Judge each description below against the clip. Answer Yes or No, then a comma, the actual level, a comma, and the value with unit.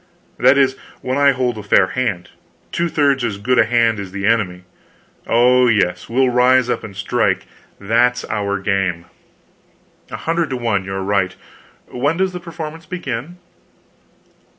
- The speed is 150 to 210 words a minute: Yes, average, 160 wpm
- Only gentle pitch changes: No, average, 5.0 semitones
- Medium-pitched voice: No, low, 120 Hz